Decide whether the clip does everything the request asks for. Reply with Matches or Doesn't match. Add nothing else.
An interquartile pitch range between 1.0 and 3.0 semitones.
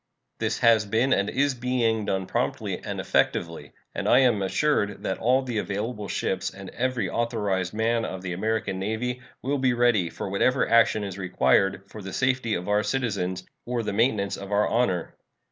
Doesn't match